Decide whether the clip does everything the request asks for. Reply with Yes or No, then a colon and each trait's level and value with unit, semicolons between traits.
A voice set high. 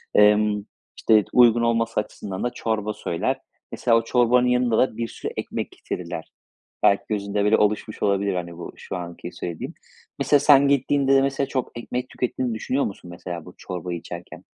No: low, 110 Hz